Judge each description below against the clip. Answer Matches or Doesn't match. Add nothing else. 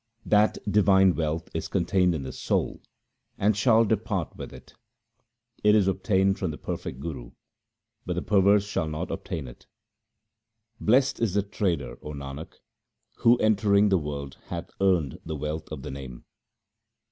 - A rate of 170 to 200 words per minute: Doesn't match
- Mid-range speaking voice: Doesn't match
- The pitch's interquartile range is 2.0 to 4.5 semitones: Doesn't match